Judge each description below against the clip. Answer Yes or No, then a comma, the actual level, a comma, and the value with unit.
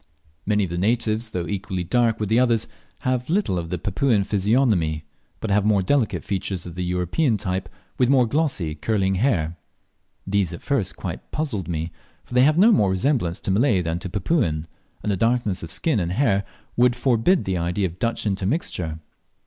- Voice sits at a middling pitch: No, low, 100 Hz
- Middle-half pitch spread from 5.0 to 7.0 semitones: Yes, average, 5.3 semitones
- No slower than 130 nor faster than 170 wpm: No, average, 190 wpm